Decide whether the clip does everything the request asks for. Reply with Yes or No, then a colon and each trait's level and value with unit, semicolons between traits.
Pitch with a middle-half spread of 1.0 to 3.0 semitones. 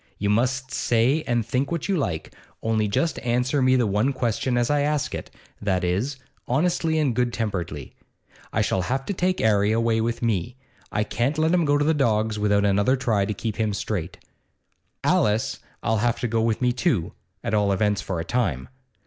No: average, 4.3 semitones